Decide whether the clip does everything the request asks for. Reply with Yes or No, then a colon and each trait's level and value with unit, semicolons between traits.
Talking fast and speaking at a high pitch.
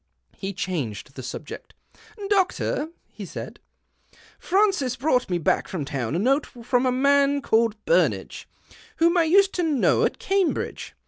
No: average, 155 wpm; very high, 270 Hz